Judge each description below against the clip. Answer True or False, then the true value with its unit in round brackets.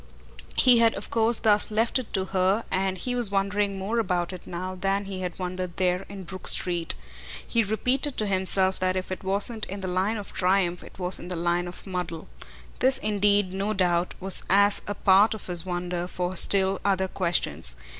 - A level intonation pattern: True (2.2 semitones)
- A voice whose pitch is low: False (190 Hz)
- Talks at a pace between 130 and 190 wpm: False (200 wpm)